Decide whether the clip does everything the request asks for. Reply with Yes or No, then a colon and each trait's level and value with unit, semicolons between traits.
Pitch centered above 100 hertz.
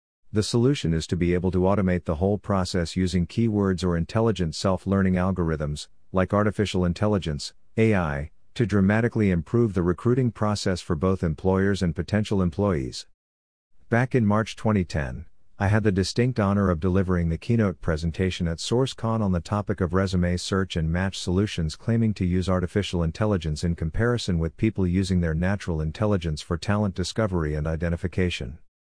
No: very low, 95 Hz